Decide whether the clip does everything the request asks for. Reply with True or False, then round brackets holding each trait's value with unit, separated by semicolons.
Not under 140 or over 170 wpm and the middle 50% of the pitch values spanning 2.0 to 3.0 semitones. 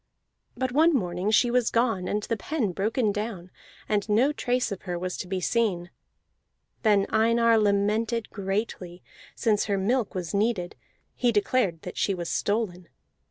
False (160 wpm; 3.8 semitones)